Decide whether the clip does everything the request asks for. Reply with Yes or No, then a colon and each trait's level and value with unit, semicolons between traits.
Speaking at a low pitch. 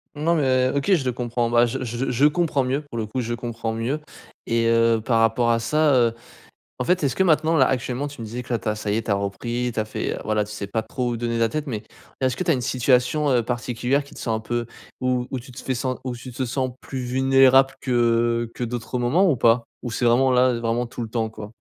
Yes: low, 120 Hz